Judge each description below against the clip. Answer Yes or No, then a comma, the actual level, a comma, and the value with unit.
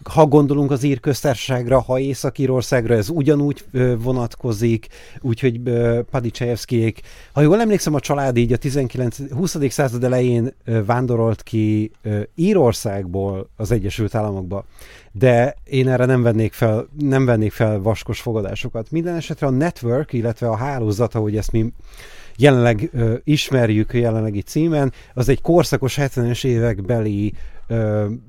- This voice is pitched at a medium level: No, low, 120 Hz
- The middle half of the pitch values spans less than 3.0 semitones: No, average, 3.5 semitones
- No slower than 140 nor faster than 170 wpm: No, average, 120 wpm